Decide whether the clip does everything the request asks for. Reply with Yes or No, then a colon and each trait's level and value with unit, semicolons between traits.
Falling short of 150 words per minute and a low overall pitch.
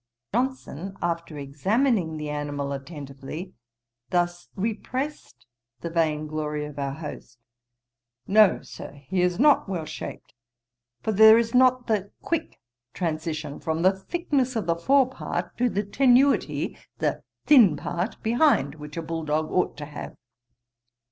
No: average, 140 wpm; medium, 175 Hz